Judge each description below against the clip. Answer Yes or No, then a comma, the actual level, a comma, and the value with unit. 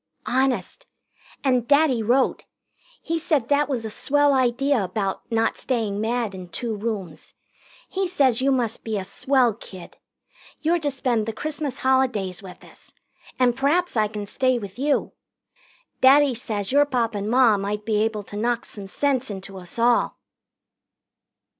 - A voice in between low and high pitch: No, high, 240 Hz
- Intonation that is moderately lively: Yes, average, 4.5 semitones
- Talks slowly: No, average, 160 wpm